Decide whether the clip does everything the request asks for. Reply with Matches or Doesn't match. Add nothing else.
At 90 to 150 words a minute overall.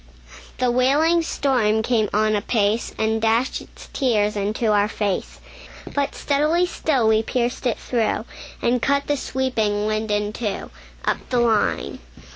Matches